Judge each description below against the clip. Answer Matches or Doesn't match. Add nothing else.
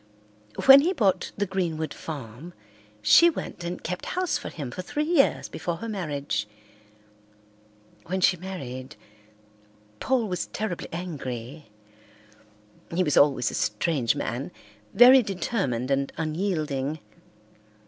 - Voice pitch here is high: Doesn't match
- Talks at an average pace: Doesn't match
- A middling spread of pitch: Doesn't match